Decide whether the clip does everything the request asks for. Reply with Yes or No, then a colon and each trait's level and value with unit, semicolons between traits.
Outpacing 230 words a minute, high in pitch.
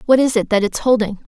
Yes: fast, 275 wpm; high, 230 Hz